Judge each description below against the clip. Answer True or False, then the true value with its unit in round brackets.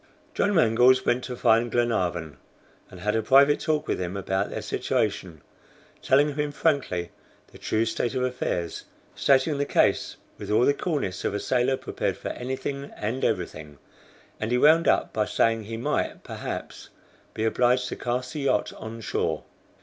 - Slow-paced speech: False (170 wpm)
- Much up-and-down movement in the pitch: False (4.5 semitones)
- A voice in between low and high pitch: False (120 Hz)